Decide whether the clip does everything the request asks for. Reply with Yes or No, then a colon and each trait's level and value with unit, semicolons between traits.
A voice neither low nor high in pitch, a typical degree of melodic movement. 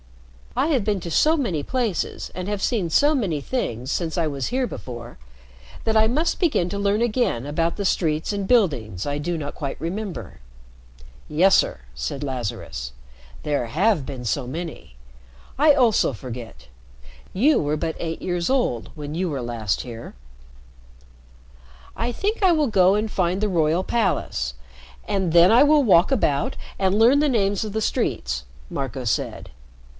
No: medium, 175 Hz; wide, 7.9 semitones